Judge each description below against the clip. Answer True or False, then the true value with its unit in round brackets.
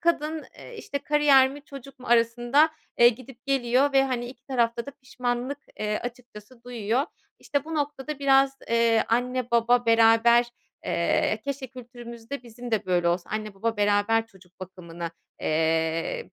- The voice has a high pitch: True (240 Hz)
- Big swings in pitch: False (3.3 semitones)